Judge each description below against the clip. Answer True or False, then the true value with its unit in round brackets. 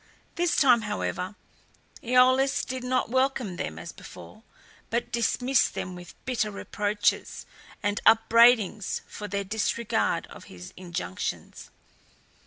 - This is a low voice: False (220 Hz)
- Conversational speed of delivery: False (115 wpm)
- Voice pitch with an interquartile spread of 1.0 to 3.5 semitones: False (4.2 semitones)